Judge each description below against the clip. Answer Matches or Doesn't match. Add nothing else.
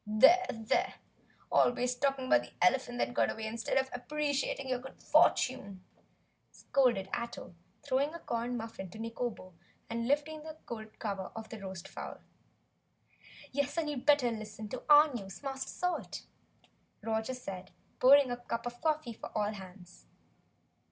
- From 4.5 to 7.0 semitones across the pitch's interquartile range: Doesn't match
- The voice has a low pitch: Doesn't match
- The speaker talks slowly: Doesn't match